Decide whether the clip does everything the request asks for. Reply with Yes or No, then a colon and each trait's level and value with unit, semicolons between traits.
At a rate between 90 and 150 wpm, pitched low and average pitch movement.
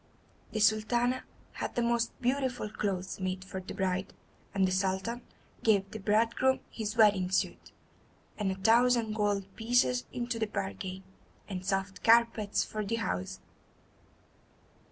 No: slow, 135 wpm; high, 210 Hz; average, 3.5 semitones